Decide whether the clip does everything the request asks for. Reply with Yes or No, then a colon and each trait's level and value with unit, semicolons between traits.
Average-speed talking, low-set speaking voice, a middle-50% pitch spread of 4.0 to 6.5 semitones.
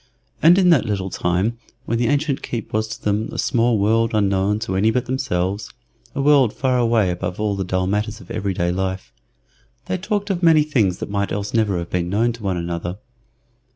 No: fast, 210 wpm; low, 105 Hz; average, 4.3 semitones